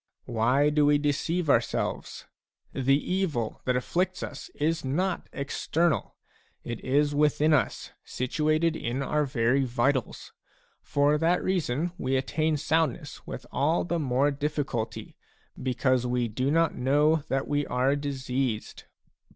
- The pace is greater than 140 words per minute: No, slow, 135 wpm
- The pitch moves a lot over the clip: No, average, 3.1 semitones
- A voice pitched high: No, medium, 145 Hz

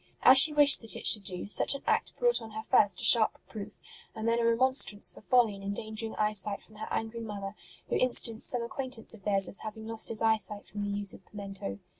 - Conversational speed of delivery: No, fast, 230 wpm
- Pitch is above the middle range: Yes, high, 220 Hz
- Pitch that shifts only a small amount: Yes, narrow, 2.3 semitones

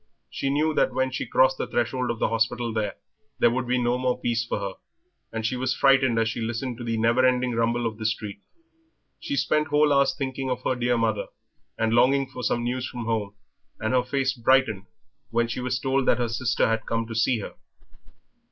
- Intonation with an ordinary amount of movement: No, narrow, 2.3 semitones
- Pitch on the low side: Yes, low, 120 Hz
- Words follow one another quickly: Yes, fast, 215 wpm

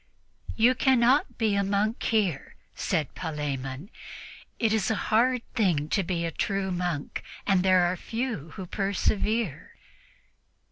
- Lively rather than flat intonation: No, average, 4.8 semitones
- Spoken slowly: Yes, slow, 130 wpm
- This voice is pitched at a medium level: No, high, 195 Hz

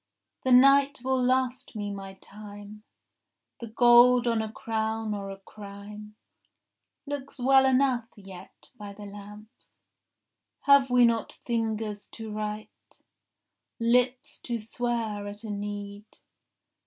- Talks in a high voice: Yes, high, 220 Hz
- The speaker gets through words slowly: Yes, slow, 125 wpm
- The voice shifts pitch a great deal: No, average, 3.2 semitones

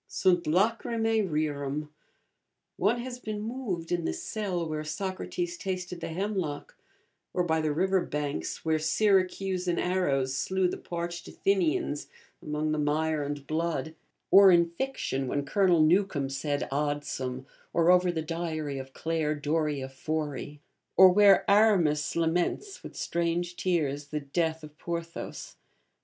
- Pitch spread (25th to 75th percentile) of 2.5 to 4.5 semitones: Yes, average, 3.9 semitones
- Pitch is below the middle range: No, medium, 165 Hz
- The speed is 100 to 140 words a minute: Yes, slow, 135 wpm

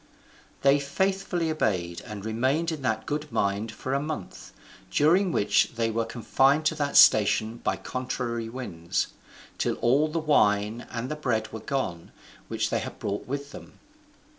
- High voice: No, low, 130 Hz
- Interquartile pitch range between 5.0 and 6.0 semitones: Yes, average, 5.3 semitones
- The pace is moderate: Yes, average, 160 wpm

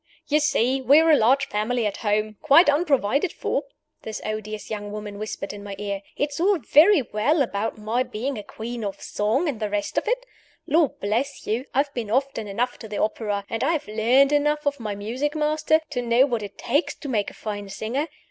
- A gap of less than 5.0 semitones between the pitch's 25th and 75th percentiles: No, average, 5.3 semitones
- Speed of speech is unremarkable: No, fast, 215 wpm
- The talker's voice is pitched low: No, high, 235 Hz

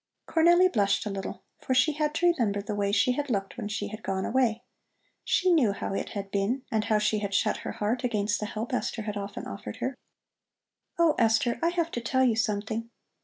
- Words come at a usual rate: No, fast, 220 wpm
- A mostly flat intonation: No, average, 4.2 semitones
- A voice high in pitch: Yes, high, 220 Hz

